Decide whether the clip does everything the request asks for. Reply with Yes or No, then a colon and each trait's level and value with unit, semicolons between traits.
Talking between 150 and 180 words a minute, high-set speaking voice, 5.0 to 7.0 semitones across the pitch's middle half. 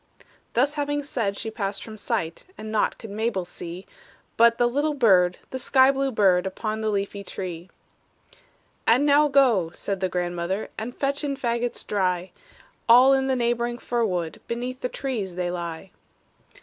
Yes: average, 165 wpm; high, 220 Hz; wide, 5.4 semitones